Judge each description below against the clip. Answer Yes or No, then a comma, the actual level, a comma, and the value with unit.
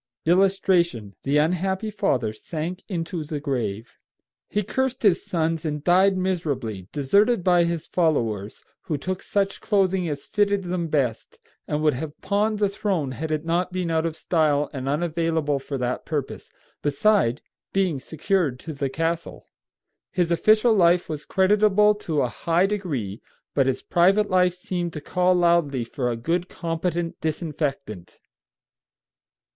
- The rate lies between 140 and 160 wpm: Yes, average, 150 wpm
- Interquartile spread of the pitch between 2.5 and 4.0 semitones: No, average, 4.5 semitones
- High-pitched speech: No, medium, 165 Hz